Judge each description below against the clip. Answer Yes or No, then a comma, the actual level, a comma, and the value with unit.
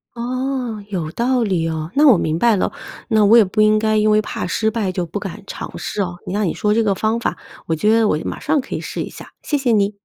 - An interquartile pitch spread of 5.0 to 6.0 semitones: No, average, 3.3 semitones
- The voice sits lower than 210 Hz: No, high, 215 Hz